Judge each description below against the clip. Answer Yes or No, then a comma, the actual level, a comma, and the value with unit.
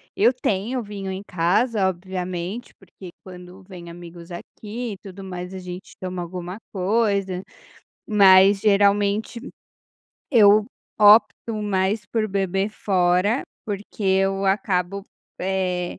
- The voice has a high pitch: Yes, high, 195 Hz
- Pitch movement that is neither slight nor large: No, narrow, 2.2 semitones